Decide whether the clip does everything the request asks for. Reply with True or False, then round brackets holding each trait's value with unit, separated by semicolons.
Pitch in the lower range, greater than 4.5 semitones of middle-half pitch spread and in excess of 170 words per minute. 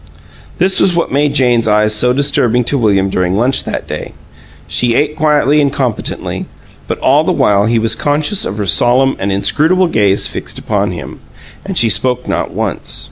True (125 Hz; 5.6 semitones; 185 wpm)